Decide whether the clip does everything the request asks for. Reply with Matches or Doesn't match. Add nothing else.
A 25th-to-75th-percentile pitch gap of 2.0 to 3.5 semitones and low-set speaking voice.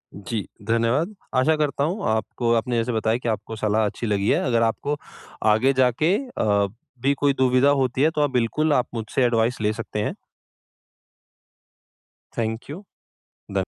Doesn't match